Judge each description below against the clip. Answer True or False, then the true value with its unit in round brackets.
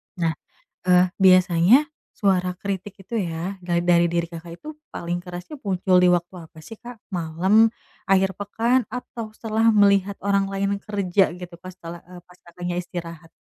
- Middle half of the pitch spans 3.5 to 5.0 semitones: False (2.5 semitones)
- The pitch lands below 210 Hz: True (185 Hz)